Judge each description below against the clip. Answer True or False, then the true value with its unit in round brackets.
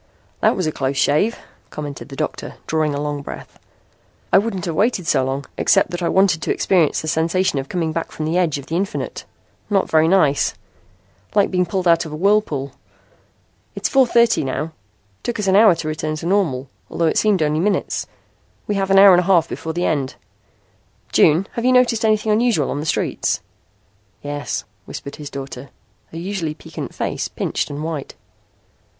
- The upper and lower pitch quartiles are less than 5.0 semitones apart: True (4.6 semitones)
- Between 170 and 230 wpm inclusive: True (190 wpm)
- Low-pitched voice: False (165 Hz)